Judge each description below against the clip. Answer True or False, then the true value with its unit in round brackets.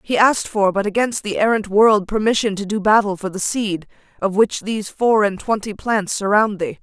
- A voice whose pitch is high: True (210 Hz)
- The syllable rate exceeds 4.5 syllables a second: True (5.2 syllables/s)